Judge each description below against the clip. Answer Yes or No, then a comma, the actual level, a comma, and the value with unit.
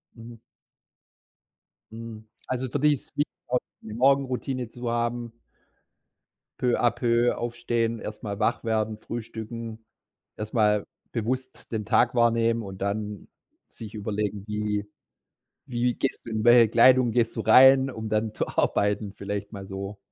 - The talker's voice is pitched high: No, low, 115 Hz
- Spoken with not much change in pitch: Yes, narrow, 2.2 semitones